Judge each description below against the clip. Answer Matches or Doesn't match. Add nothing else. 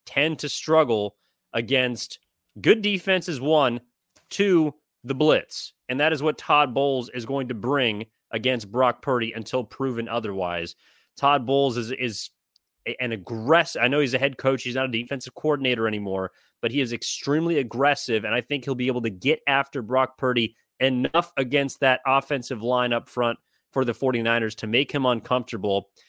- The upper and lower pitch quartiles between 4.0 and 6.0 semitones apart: Doesn't match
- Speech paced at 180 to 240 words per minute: Doesn't match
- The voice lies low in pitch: Matches